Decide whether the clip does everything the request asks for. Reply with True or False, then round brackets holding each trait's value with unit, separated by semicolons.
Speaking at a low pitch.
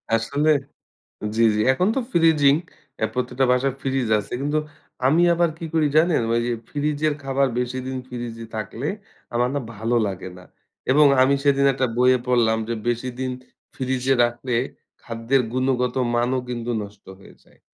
True (130 Hz)